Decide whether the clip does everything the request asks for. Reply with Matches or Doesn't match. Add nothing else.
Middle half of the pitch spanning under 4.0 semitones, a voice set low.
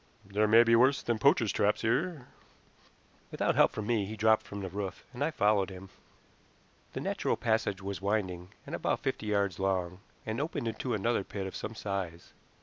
Matches